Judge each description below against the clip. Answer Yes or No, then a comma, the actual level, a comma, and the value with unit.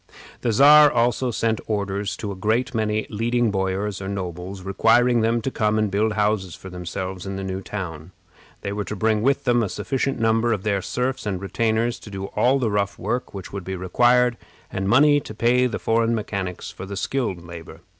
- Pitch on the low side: Yes, low, 105 Hz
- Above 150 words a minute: Yes, fast, 205 wpm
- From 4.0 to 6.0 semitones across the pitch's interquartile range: No, average, 3.5 semitones